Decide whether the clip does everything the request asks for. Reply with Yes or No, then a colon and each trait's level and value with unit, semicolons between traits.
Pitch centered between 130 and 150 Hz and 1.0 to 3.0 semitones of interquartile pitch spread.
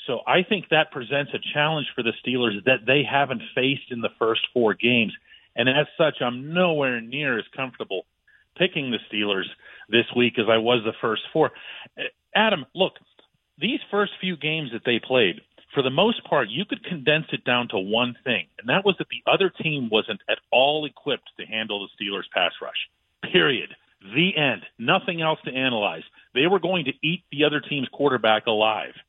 No: medium, 140 Hz; average, 5.1 semitones